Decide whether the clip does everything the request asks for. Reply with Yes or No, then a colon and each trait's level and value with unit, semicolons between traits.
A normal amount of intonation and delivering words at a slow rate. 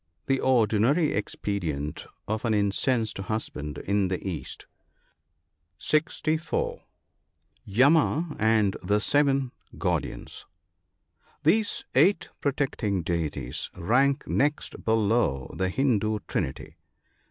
No: wide, 6.3 semitones; slow, 95 wpm